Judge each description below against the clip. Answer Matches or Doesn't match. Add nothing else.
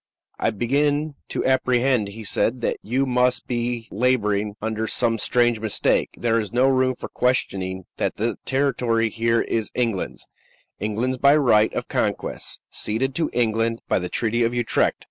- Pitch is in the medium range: Doesn't match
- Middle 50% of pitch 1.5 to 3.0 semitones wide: Matches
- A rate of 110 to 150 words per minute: Doesn't match